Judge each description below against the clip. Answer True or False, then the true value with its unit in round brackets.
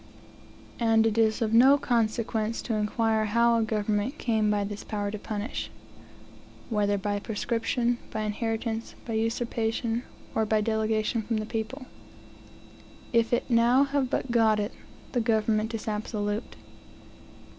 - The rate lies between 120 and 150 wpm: True (140 wpm)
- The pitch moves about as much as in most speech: False (1.5 semitones)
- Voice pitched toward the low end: False (225 Hz)